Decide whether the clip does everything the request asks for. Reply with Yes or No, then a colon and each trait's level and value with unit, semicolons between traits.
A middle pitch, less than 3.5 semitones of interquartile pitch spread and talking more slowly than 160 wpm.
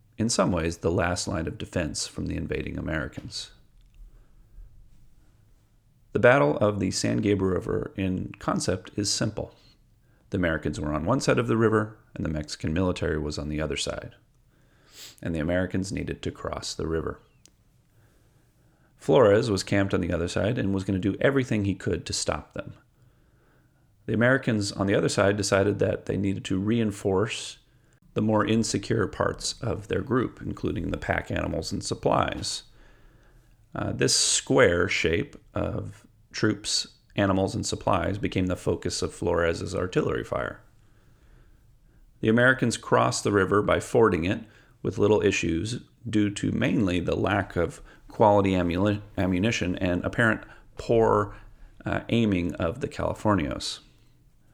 No: low, 100 Hz; average, 3.1 semitones; average, 150 wpm